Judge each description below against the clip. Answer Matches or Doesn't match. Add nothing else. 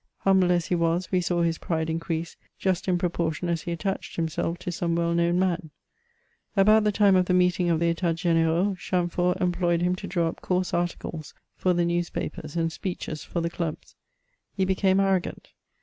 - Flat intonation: Matches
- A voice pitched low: Doesn't match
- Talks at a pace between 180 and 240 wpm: Matches